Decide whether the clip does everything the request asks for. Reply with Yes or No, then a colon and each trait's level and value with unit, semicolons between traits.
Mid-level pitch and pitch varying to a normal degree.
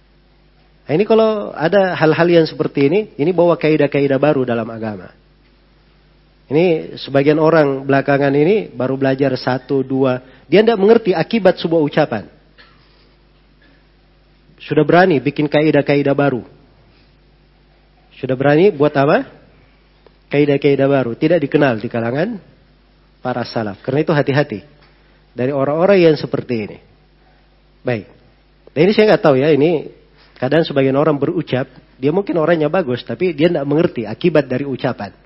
Yes: medium, 145 Hz; average, 3.7 semitones